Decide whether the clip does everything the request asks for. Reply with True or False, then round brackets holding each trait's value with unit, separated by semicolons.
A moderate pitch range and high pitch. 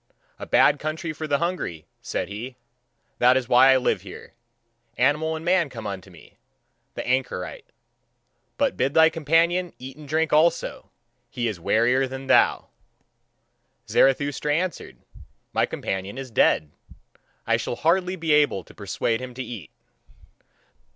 False (4.6 semitones; 135 Hz)